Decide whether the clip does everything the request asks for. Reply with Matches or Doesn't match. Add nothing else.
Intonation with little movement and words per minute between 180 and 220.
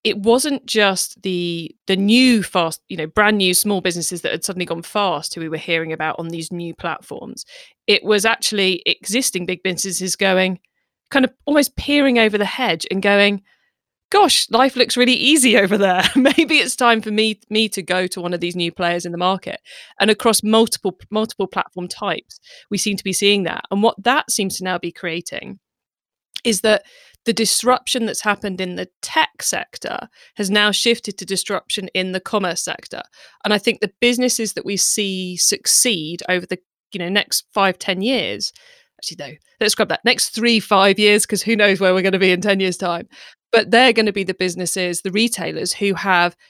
Doesn't match